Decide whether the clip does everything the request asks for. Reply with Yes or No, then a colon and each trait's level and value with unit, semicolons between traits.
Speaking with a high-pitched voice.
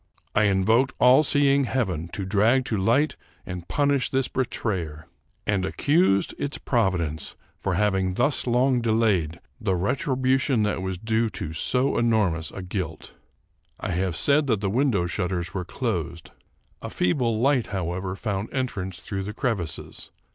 No: low, 105 Hz